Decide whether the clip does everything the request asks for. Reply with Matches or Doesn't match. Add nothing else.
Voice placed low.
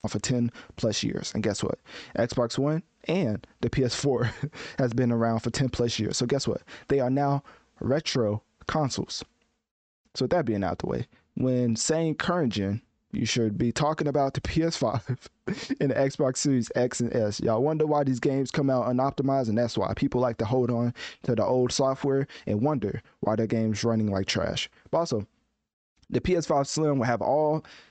Matches